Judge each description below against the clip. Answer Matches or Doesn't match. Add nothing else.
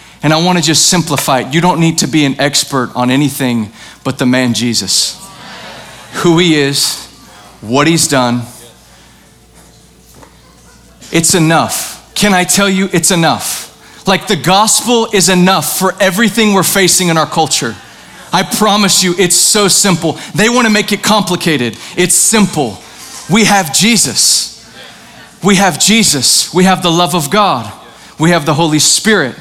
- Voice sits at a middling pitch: Matches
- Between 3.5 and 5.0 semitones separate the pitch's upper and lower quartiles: Doesn't match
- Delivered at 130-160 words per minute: Matches